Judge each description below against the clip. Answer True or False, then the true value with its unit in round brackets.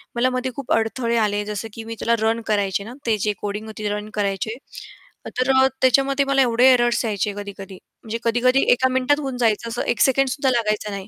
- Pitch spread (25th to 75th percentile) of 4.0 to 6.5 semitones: False (3.4 semitones)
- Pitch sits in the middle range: False (230 Hz)